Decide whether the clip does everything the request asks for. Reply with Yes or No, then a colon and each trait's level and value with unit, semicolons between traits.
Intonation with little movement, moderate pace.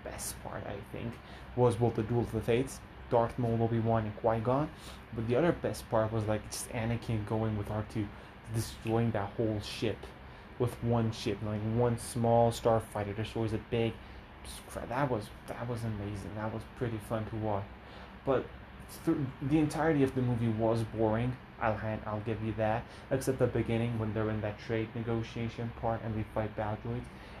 Yes: narrow, 1.5 semitones; average, 180 wpm